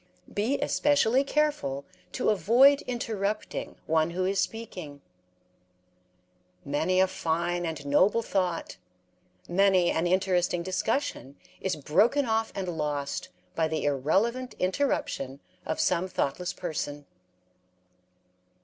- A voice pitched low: No, medium, 185 Hz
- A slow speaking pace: Yes, slow, 105 wpm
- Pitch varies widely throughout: Yes, wide, 5.8 semitones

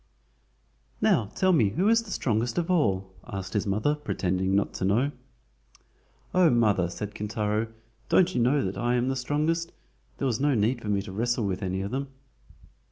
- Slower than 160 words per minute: No, average, 185 wpm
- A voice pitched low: Yes, low, 115 Hz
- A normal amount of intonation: No, wide, 6.4 semitones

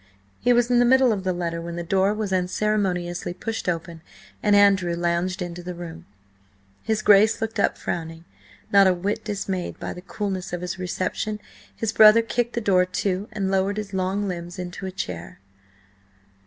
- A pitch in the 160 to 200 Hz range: Yes, high, 190 Hz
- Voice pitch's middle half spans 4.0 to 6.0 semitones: No, average, 3.1 semitones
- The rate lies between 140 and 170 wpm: No, average, 180 wpm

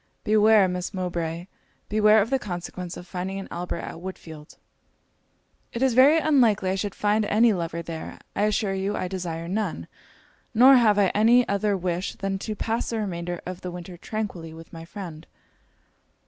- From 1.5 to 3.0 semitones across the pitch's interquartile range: No, average, 3.5 semitones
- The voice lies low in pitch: No, high, 190 Hz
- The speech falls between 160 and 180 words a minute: Yes, average, 175 wpm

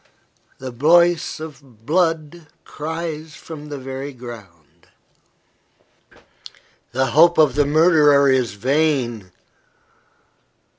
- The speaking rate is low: Yes, slow, 90 wpm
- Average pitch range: Yes, average, 3.7 semitones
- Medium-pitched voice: Yes, medium, 145 Hz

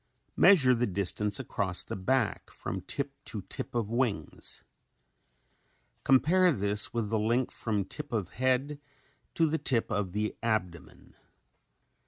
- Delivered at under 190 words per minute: Yes, slow, 135 wpm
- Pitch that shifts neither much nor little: Yes, average, 4.5 semitones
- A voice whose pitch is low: Yes, low, 115 Hz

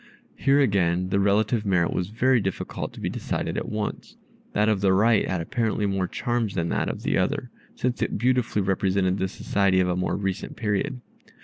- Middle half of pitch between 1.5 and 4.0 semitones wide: Yes, average, 3.0 semitones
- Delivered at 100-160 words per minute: No, average, 195 wpm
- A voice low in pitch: Yes, low, 100 Hz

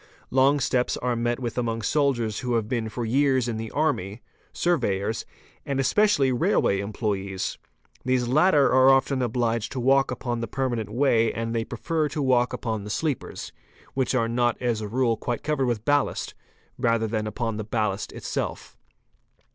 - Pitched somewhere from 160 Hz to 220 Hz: No, low, 120 Hz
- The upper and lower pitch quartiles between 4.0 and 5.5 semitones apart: No, average, 3.0 semitones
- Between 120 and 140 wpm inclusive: No, average, 170 wpm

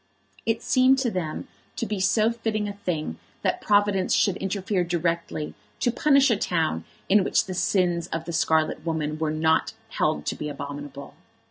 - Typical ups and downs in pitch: Yes, average, 5.0 semitones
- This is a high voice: No, medium, 180 Hz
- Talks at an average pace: Yes, average, 170 wpm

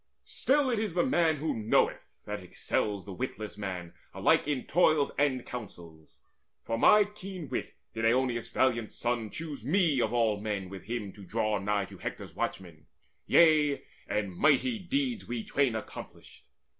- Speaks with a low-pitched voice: Yes, low, 120 Hz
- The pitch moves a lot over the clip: Yes, wide, 7.2 semitones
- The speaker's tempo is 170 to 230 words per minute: No, average, 160 wpm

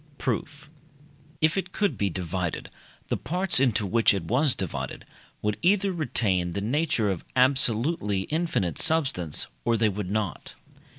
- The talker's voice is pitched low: Yes, low, 115 Hz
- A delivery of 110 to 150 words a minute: Yes, average, 140 wpm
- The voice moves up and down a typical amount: No, wide, 8.2 semitones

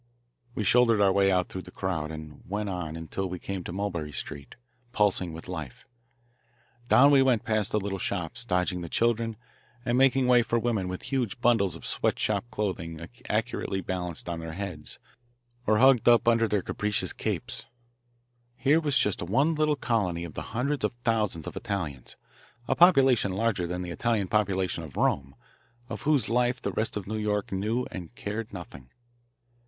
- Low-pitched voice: Yes, low, 100 Hz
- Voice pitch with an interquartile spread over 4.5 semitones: Yes, average, 4.9 semitones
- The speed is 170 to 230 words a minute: Yes, average, 175 wpm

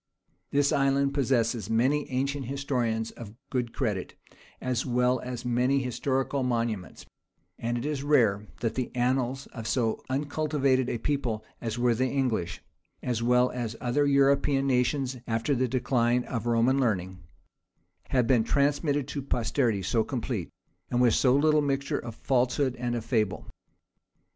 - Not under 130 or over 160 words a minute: Yes, average, 150 wpm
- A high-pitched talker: No, low, 125 Hz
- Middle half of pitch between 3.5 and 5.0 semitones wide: No, average, 2.8 semitones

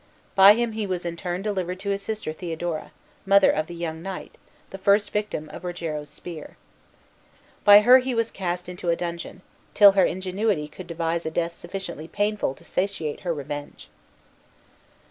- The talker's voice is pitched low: No, medium, 180 Hz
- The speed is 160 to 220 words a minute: Yes, average, 170 wpm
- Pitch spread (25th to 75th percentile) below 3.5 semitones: Yes, average, 3.1 semitones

